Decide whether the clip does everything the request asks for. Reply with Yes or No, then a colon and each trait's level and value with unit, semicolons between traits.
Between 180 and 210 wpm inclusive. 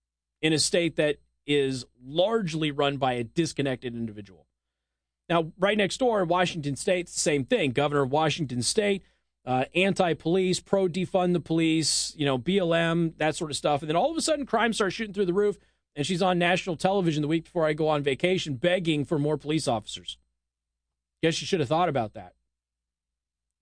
Yes: average, 190 wpm